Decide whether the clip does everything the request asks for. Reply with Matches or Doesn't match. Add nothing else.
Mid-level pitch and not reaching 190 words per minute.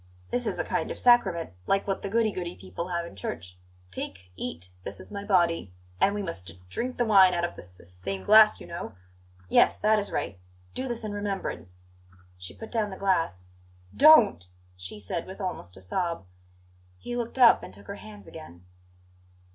Doesn't match